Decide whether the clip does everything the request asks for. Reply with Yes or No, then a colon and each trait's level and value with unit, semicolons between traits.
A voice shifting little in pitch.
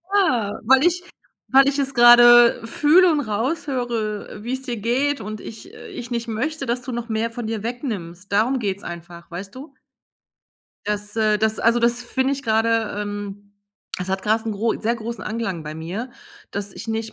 No: average, 3.2 semitones